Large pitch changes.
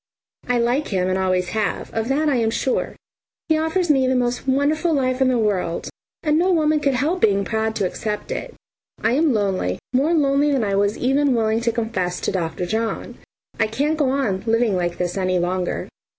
Yes: wide, 6.1 semitones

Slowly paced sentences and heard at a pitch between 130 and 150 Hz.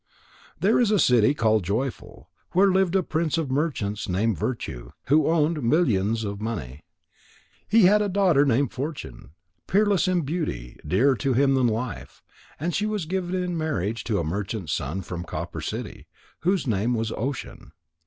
No: average, 165 wpm; low, 135 Hz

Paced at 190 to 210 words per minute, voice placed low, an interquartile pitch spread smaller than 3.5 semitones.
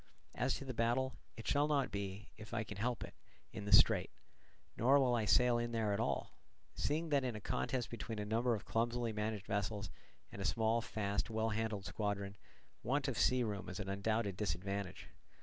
Yes: average, 200 wpm; low, 110 Hz; average, 3.1 semitones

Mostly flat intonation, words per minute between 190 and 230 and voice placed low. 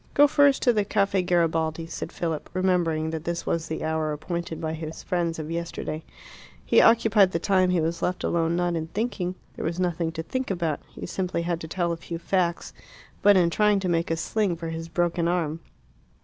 No: narrow, 2.1 semitones; fast, 205 wpm; medium, 170 Hz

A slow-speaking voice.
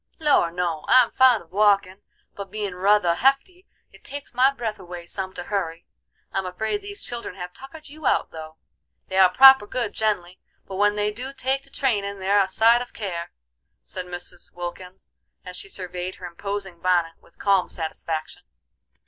No: average, 175 wpm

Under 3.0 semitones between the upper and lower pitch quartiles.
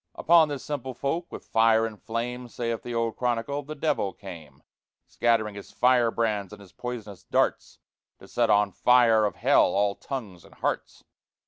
No: average, 3.3 semitones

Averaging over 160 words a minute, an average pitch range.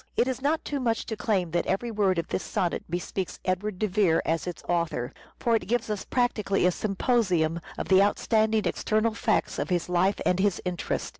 Yes: fast, 205 wpm; average, 3.8 semitones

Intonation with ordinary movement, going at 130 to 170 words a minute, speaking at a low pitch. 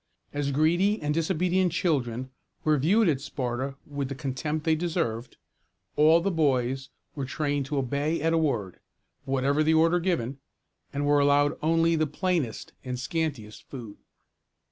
No: average, 3.5 semitones; average, 150 wpm; medium, 145 Hz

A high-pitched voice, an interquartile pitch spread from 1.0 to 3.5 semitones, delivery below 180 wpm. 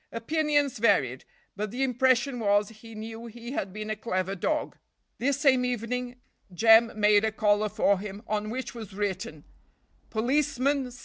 Yes: high, 225 Hz; average, 3.2 semitones; average, 160 wpm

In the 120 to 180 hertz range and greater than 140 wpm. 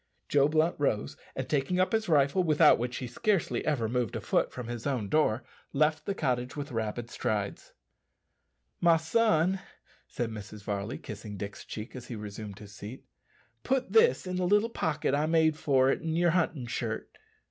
Yes: medium, 140 Hz; average, 180 wpm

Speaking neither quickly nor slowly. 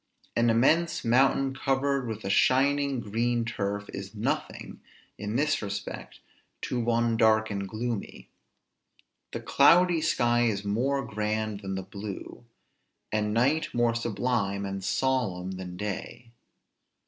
No: slow, 125 wpm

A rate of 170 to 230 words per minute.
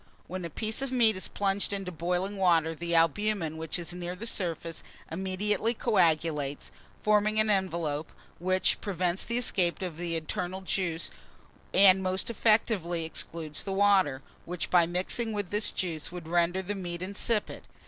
No: average, 160 wpm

